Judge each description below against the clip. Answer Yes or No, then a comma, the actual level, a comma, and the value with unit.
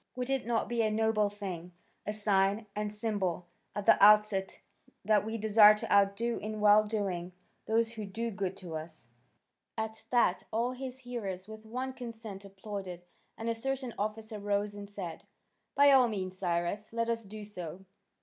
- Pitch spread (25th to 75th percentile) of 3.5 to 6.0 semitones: No, narrow, 2.6 semitones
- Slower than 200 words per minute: Yes, average, 170 wpm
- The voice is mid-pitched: No, high, 210 Hz